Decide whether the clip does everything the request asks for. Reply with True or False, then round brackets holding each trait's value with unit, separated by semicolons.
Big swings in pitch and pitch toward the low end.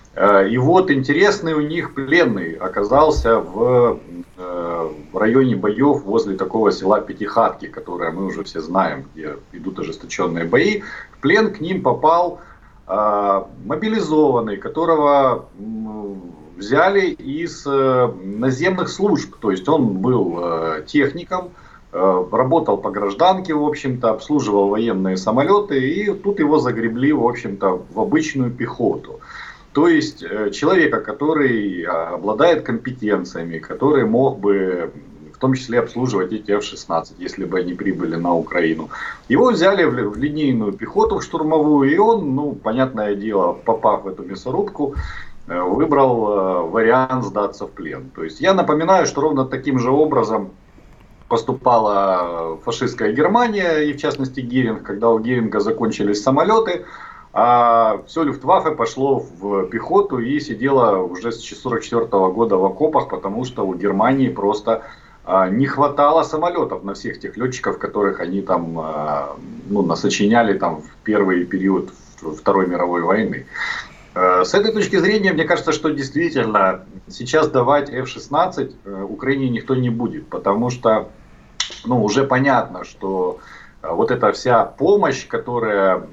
True (7.0 semitones; 120 Hz)